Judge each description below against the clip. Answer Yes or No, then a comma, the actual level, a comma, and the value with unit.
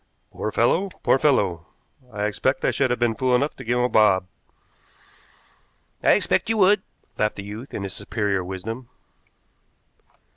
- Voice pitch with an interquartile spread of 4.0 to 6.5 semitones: Yes, average, 4.4 semitones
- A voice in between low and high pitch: No, low, 115 Hz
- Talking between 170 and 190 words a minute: No, average, 160 wpm